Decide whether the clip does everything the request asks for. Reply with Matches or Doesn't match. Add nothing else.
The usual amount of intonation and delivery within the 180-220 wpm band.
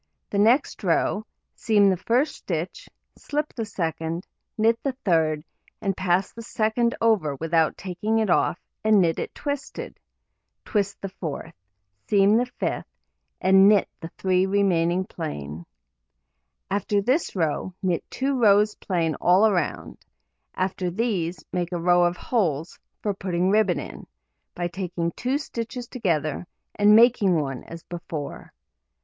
Doesn't match